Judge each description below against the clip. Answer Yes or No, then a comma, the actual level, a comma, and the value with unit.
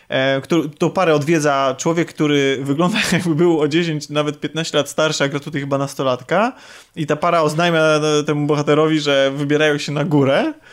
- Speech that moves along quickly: Yes, fast, 170 wpm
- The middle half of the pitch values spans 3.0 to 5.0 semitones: No, narrow, 2.5 semitones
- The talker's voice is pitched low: No, medium, 150 Hz